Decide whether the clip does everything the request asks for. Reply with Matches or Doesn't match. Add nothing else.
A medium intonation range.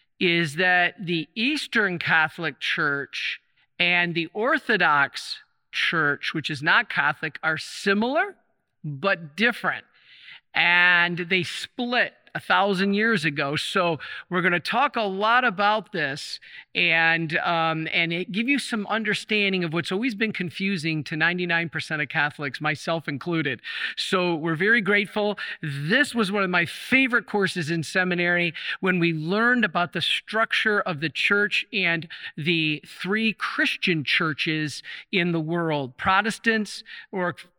Matches